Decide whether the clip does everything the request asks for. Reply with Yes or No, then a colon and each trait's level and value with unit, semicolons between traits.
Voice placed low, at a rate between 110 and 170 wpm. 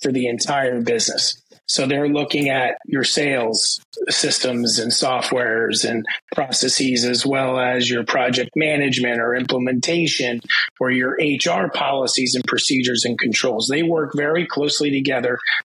Yes: low, 130 Hz; average, 140 wpm